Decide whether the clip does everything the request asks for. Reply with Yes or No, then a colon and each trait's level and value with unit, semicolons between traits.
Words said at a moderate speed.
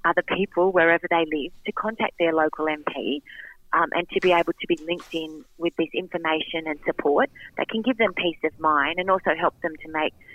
No: fast, 215 wpm